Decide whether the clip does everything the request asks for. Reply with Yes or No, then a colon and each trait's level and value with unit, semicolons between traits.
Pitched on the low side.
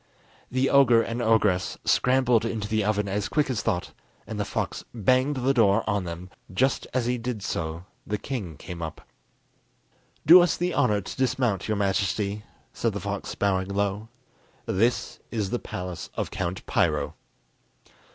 Yes: low, 105 Hz